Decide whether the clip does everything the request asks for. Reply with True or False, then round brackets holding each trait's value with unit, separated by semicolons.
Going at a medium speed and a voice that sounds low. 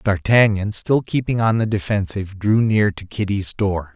True (180 wpm; 100 Hz)